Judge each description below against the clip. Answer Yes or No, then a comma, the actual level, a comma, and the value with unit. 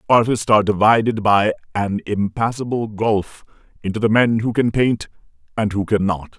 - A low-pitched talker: Yes, low, 105 Hz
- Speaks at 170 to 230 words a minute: No, average, 150 wpm